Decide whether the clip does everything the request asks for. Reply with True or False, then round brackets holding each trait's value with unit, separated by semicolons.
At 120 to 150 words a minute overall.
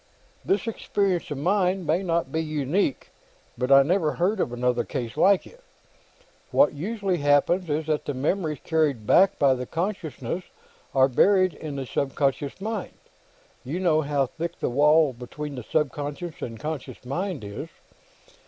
False (160 wpm)